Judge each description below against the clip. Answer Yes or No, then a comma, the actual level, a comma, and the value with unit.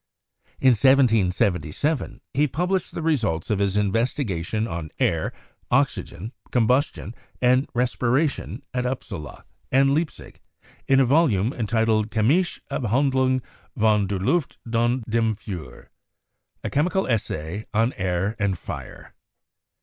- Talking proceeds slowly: Yes, slow, 115 wpm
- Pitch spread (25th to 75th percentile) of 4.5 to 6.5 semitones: Yes, average, 4.8 semitones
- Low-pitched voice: Yes, low, 115 Hz